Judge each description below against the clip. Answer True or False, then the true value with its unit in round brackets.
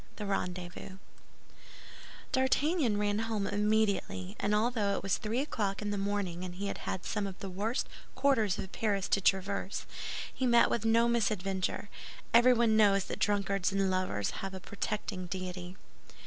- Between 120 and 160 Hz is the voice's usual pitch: False (200 Hz)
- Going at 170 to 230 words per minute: False (155 wpm)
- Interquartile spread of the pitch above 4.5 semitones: False (2.7 semitones)